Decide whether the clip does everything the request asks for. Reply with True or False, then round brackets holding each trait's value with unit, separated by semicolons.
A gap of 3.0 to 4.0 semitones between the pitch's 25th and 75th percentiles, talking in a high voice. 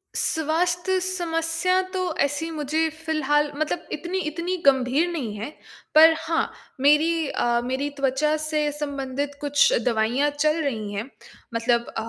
True (3.5 semitones; 295 Hz)